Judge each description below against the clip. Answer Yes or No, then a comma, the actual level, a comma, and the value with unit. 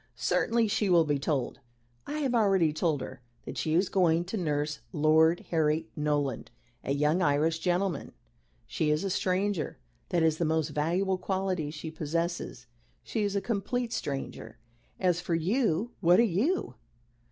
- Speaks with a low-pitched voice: No, medium, 170 Hz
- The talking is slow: No, average, 160 wpm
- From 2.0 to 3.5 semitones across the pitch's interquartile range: No, average, 4.2 semitones